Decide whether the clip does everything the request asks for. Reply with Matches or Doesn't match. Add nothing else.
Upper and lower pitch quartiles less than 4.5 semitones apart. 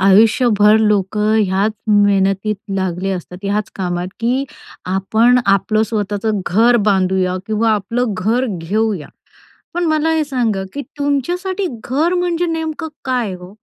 Doesn't match